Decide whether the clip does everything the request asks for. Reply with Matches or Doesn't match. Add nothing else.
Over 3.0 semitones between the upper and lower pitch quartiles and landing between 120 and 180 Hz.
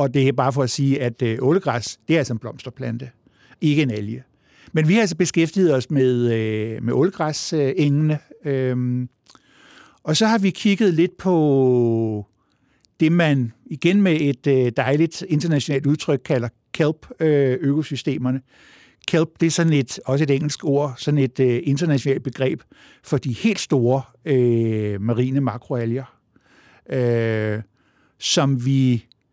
Matches